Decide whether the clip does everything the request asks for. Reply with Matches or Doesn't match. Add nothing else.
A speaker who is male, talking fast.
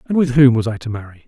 Matches